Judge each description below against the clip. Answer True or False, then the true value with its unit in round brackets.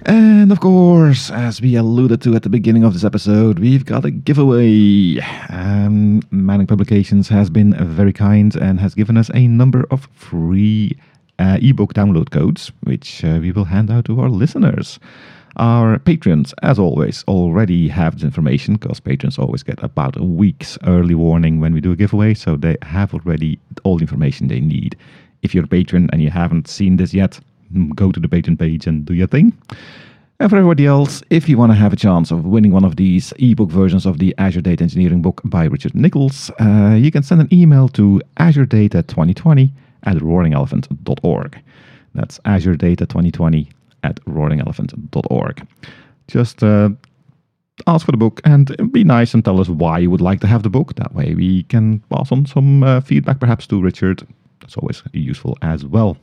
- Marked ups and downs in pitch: True (6.3 semitones)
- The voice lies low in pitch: True (105 Hz)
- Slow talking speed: False (190 wpm)